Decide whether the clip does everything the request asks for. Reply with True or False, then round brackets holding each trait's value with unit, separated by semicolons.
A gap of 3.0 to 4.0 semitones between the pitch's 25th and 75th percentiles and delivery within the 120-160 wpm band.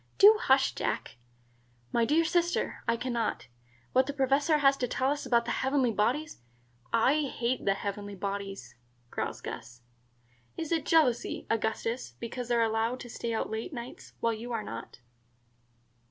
False (3.7 semitones; 170 wpm)